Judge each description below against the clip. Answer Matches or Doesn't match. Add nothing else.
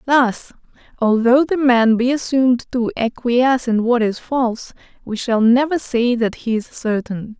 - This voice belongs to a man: Doesn't match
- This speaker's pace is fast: Doesn't match